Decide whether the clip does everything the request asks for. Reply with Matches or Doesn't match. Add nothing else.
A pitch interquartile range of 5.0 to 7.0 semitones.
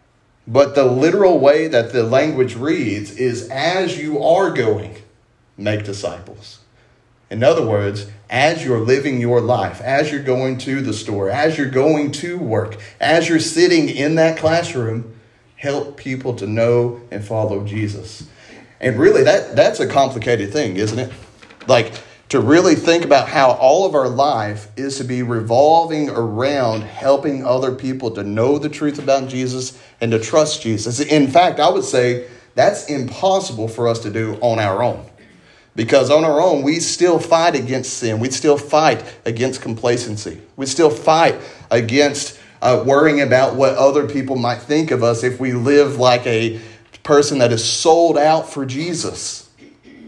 Doesn't match